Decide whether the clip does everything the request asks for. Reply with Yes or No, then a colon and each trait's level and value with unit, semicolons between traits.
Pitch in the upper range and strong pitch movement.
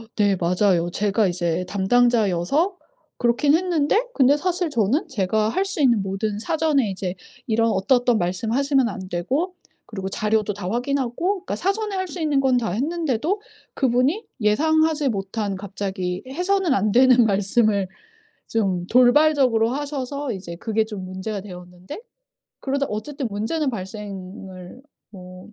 Yes: high, 225 Hz; wide, 6.6 semitones